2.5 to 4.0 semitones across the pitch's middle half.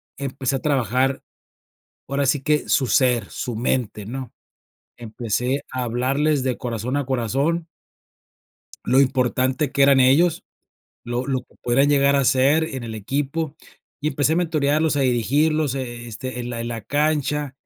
Yes: average, 2.8 semitones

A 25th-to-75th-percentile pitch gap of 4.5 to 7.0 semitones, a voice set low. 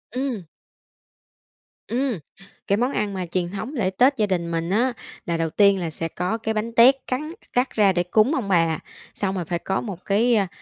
No: average, 5.1 semitones; high, 200 Hz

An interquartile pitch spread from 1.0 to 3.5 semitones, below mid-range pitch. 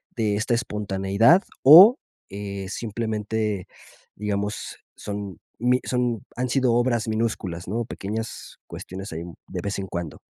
Yes: average, 3.1 semitones; low, 105 Hz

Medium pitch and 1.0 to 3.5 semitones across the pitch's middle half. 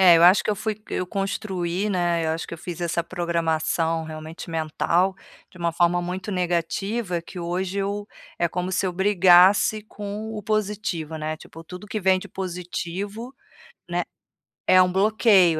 Yes: medium, 180 Hz; average, 2.9 semitones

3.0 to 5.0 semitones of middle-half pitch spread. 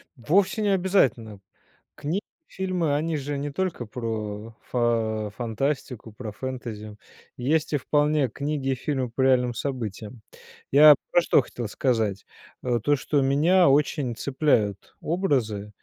Yes: average, 4.7 semitones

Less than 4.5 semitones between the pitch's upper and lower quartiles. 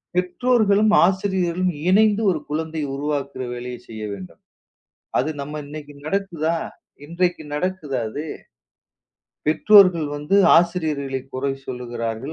No: average, 4.8 semitones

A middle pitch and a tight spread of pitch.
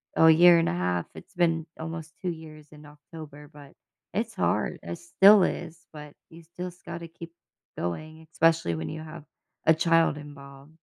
Yes: medium, 160 Hz; narrow, 2.2 semitones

